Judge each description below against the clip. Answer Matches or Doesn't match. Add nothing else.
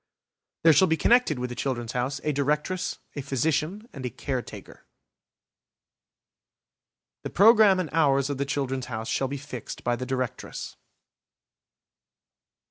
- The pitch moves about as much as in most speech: Matches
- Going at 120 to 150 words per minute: Matches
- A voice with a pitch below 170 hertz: Matches